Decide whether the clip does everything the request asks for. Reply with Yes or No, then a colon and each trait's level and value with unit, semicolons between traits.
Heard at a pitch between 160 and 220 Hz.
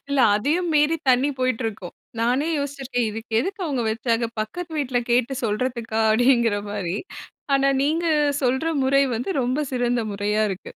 No: high, 245 Hz